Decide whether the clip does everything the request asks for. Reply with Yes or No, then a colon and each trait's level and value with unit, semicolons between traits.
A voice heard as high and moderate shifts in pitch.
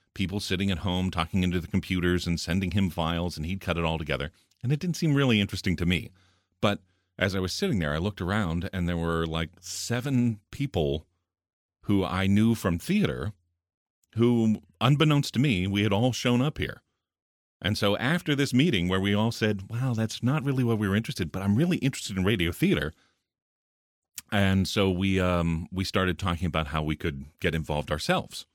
No: very low, 95 Hz; average, 4.2 semitones